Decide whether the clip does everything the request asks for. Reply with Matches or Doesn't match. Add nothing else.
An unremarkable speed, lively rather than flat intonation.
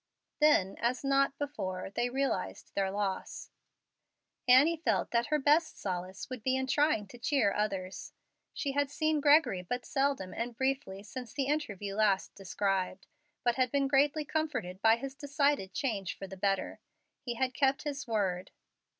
Matches